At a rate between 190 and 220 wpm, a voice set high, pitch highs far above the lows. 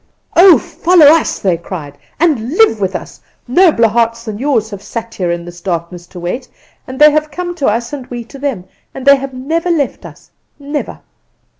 Yes: average, 195 wpm; high, 245 Hz; wide, 6.9 semitones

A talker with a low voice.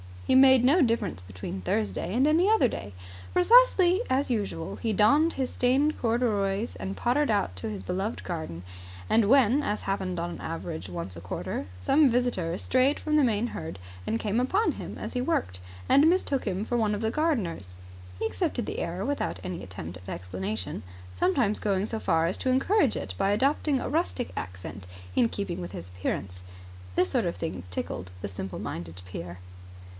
No: high, 205 Hz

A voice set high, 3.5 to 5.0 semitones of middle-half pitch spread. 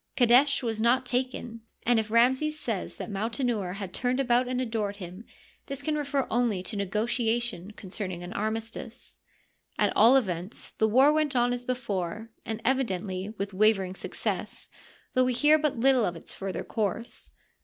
Yes: high, 230 Hz; average, 3.9 semitones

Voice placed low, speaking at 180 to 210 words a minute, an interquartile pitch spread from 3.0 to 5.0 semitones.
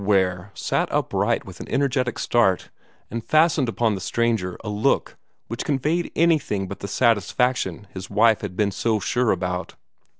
No: low, 110 Hz; average, 160 wpm; average, 4.5 semitones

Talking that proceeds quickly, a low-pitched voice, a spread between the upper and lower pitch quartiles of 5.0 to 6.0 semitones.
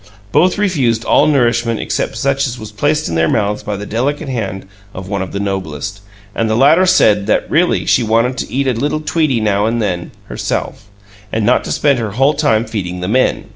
Yes: fast, 210 wpm; low, 115 Hz; average, 5.3 semitones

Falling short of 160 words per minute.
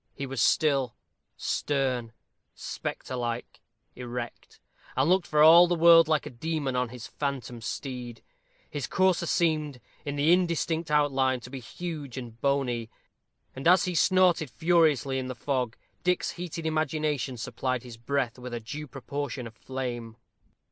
Yes: average, 150 wpm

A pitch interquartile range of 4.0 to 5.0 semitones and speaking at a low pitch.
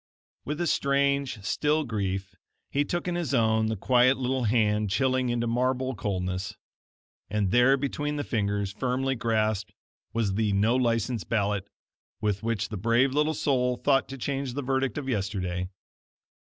Yes: average, 4.4 semitones; low, 120 Hz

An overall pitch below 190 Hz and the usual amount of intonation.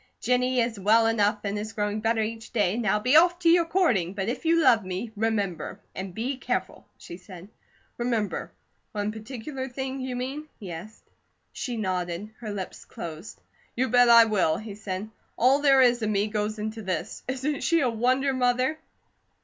No: high, 225 Hz; average, 3.7 semitones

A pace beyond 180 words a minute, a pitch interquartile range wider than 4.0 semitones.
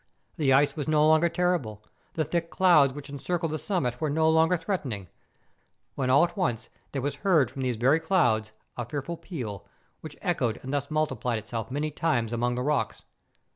Yes: average, 190 wpm; average, 4.8 semitones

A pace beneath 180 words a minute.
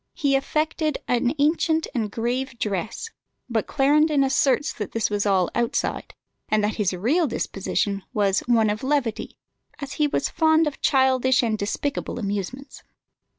Yes: average, 150 wpm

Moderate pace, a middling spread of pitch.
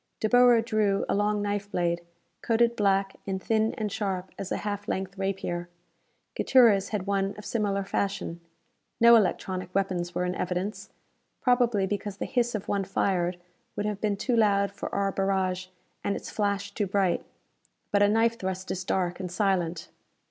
No: average, 170 wpm; narrow, 2.0 semitones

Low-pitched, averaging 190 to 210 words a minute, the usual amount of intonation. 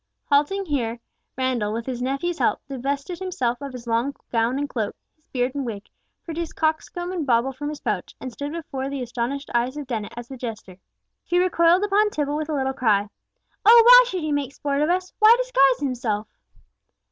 No: very high, 275 Hz; average, 195 wpm; average, 4.9 semitones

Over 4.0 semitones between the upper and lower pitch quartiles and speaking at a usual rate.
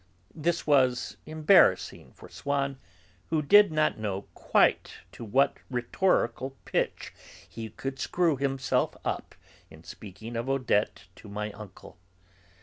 No: wide, 5.4 semitones; slow, 125 wpm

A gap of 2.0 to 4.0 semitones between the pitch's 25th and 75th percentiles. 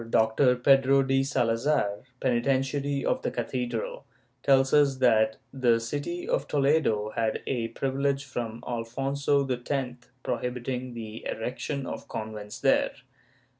Yes: average, 3.1 semitones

